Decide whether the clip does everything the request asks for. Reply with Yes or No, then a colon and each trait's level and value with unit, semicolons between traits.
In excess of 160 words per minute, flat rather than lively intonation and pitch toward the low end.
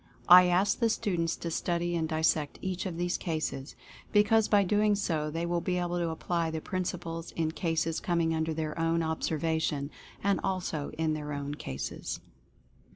No: average, 180 wpm; narrow, 2.1 semitones; medium, 165 Hz